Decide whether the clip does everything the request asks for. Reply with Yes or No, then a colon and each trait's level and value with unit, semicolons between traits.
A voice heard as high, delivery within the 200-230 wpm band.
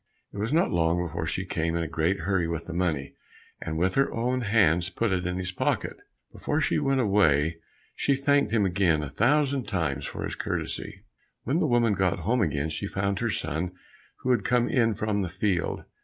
No: very low, 95 Hz; fast, 205 wpm